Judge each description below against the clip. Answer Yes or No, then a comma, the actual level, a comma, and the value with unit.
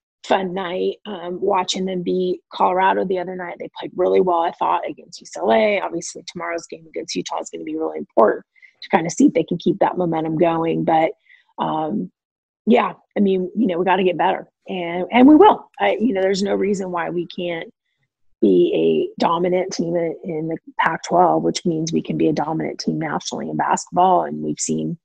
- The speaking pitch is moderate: Yes, medium, 180 Hz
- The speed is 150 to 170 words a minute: No, fast, 205 wpm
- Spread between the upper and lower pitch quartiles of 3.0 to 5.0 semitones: No, narrow, 2.6 semitones